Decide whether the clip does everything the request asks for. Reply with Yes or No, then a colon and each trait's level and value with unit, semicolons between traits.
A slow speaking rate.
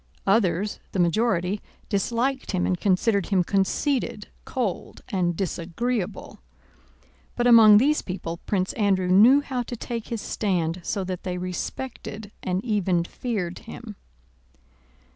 Yes: slow, 125 wpm